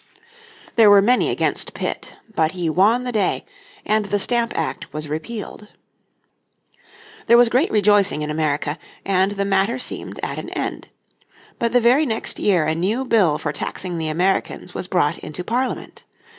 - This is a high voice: Yes, high, 200 Hz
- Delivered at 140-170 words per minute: Yes, average, 165 wpm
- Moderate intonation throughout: No, wide, 5.7 semitones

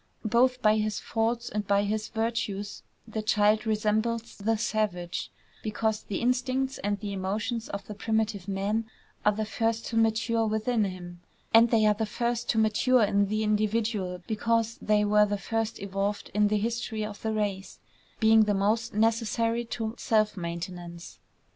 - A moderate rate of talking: Yes, average, 165 wpm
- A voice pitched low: No, high, 215 Hz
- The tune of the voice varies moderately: No, narrow, 1.8 semitones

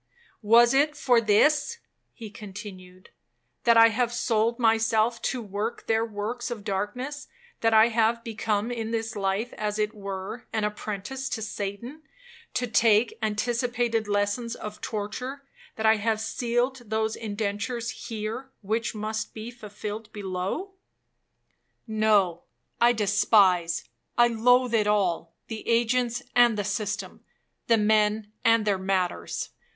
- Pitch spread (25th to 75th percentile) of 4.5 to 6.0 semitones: No, narrow, 2.4 semitones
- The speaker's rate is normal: No, slow, 125 wpm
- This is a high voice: Yes, high, 220 Hz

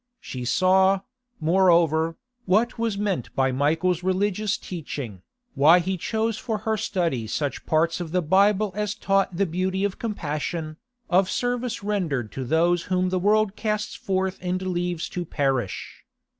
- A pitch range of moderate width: Yes, average, 3.9 semitones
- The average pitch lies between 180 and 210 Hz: Yes, medium, 185 Hz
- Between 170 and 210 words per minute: No, average, 150 wpm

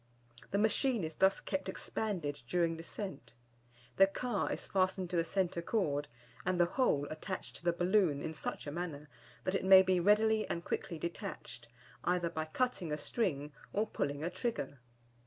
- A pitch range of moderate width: Yes, average, 3.9 semitones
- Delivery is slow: No, average, 175 wpm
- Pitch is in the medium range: Yes, medium, 180 Hz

